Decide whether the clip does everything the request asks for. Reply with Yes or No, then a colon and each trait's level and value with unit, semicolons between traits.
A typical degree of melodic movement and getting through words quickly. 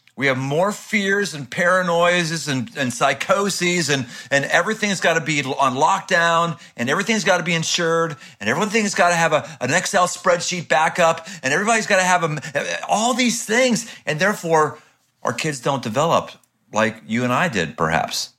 No: average, 5.0 semitones; average, 175 wpm